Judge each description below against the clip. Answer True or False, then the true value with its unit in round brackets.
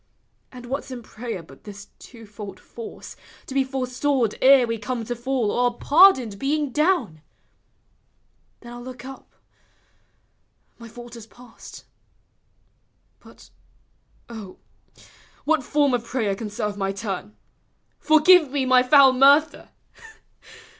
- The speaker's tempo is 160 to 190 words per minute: False (135 wpm)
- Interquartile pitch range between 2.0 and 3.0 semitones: False (3.6 semitones)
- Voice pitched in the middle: False (245 Hz)